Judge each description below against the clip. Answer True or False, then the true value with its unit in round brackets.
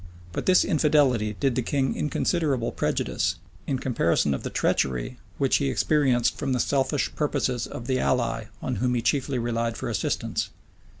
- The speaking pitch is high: False (130 Hz)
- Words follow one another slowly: False (165 wpm)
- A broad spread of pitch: False (3.3 semitones)